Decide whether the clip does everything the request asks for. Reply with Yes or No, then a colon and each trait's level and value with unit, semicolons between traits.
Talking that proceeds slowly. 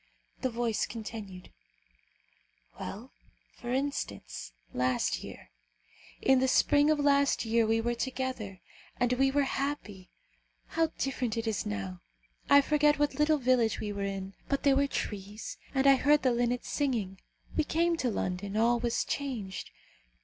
No: average, 150 wpm